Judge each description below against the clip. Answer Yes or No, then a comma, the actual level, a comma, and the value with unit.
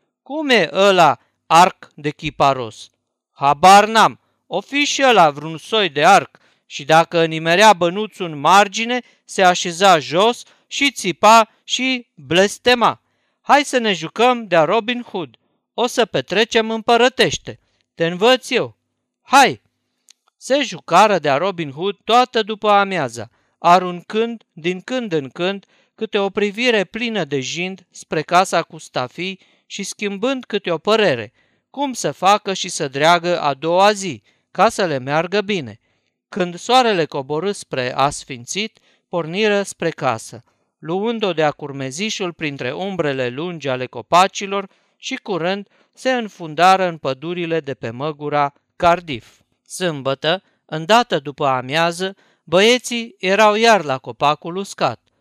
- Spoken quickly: No, average, 135 wpm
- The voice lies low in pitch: No, medium, 180 Hz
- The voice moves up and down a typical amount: No, wide, 6.2 semitones